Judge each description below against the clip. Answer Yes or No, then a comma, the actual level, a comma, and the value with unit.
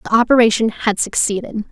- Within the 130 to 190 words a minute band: Yes, average, 140 wpm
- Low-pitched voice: No, high, 220 Hz